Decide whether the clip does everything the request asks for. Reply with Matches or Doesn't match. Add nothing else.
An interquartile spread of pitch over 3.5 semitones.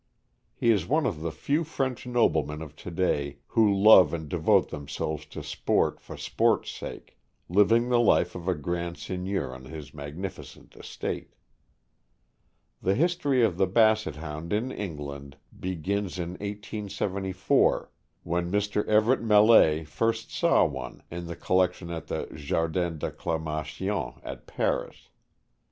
Matches